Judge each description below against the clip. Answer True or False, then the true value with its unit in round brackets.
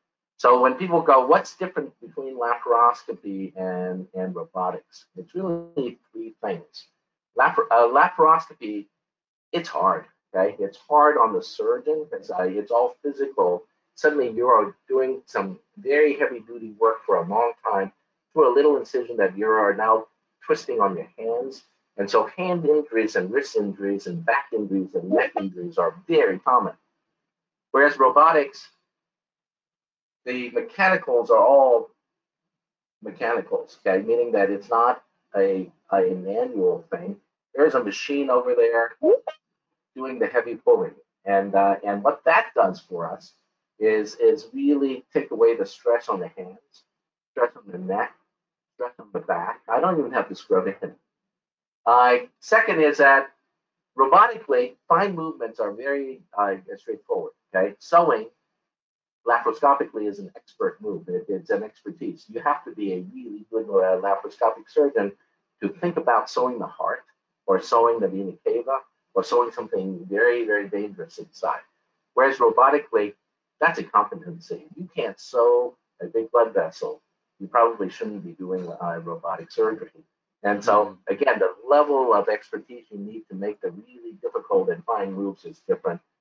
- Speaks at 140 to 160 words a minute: True (155 wpm)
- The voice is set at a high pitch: False (170 Hz)